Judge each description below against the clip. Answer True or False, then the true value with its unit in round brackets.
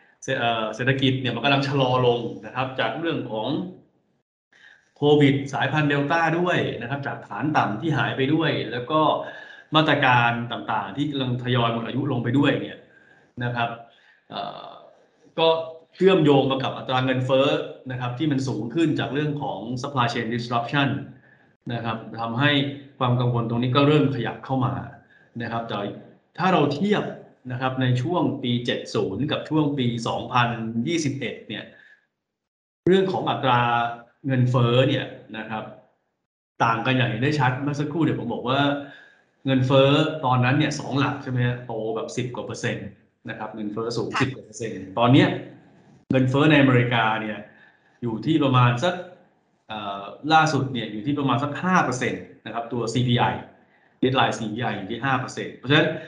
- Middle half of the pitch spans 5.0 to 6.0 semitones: False (3.5 semitones)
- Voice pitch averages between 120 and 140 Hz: True (130 Hz)